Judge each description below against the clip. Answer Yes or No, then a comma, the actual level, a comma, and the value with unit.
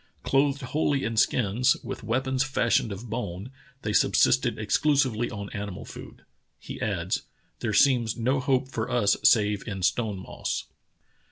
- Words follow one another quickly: No, average, 145 wpm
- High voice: No, low, 115 Hz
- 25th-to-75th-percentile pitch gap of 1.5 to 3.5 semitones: No, average, 4.0 semitones